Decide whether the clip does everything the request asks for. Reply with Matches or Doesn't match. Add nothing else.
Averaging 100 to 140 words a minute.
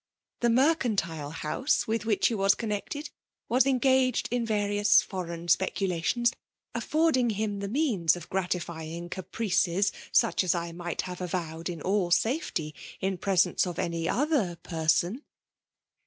Matches